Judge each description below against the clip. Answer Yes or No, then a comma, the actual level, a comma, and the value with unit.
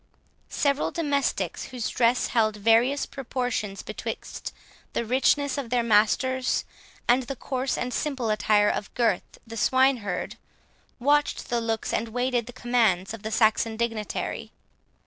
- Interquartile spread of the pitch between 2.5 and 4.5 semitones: Yes, average, 2.9 semitones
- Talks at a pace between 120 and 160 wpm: Yes, average, 140 wpm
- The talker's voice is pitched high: Yes, high, 240 Hz